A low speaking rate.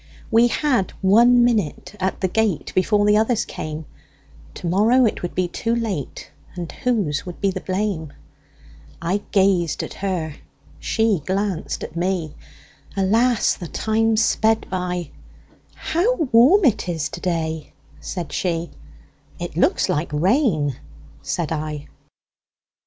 Yes: slow, 115 wpm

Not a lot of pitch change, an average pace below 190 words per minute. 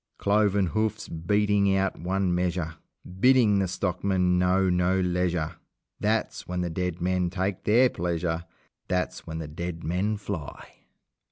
Yes: narrow, 2.3 semitones; average, 140 wpm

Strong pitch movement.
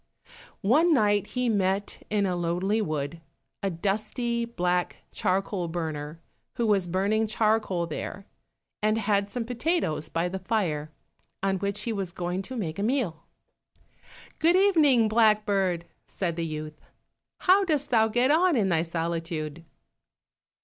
No: average, 4.8 semitones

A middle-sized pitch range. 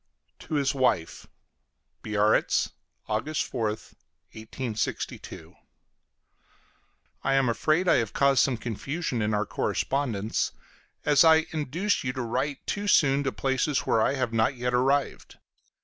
Yes: average, 4.1 semitones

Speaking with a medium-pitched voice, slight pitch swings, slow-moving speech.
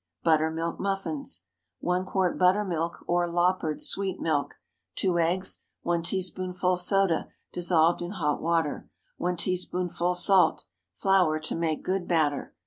Yes: medium, 175 Hz; narrow, 2.1 semitones; slow, 125 wpm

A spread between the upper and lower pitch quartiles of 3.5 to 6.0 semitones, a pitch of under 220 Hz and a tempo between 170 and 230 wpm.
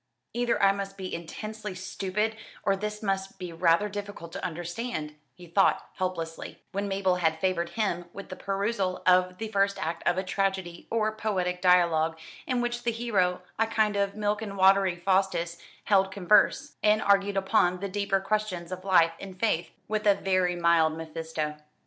No: average, 2.7 semitones; high, 190 Hz; average, 175 wpm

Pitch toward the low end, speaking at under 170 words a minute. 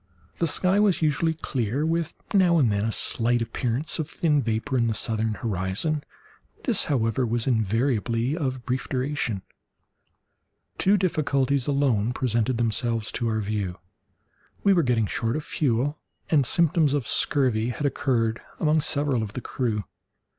Yes: low, 130 Hz; average, 145 wpm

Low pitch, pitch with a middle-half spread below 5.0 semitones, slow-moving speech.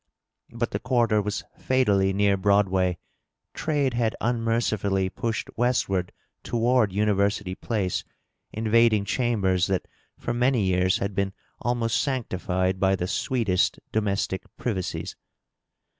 Yes: low, 105 Hz; average, 3.6 semitones; slow, 115 wpm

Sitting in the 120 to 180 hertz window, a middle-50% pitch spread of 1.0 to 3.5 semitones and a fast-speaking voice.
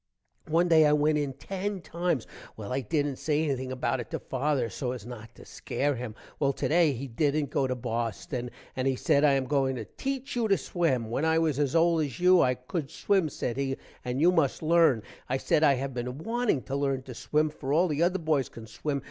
No: medium, 140 Hz; average, 4.0 semitones; fast, 230 wpm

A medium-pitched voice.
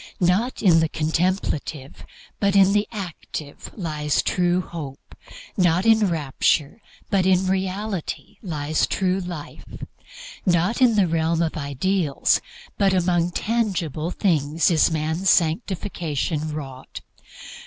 Yes: medium, 175 Hz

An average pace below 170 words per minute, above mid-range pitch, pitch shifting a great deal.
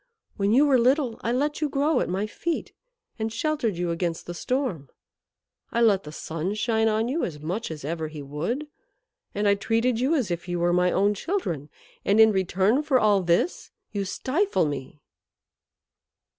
No: average, 185 wpm; high, 210 Hz; wide, 6.6 semitones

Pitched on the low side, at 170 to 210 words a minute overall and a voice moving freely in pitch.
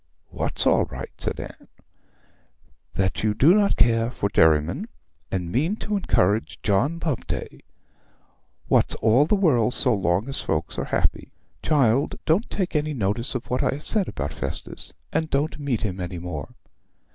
No: low, 120 Hz; average, 160 wpm; wide, 7.9 semitones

